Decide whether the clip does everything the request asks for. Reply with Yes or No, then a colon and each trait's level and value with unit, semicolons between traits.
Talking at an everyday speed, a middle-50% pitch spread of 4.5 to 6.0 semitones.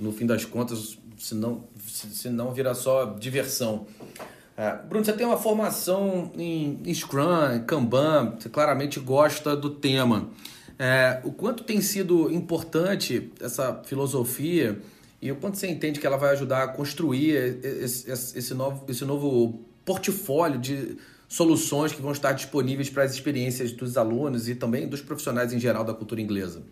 No: average, 160 wpm; average, 4.1 semitones